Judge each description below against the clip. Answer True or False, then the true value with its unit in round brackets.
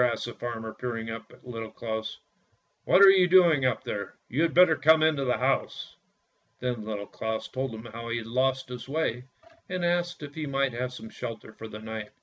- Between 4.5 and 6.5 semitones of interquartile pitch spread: True (4.8 semitones)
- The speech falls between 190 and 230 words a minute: True (205 wpm)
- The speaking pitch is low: True (125 Hz)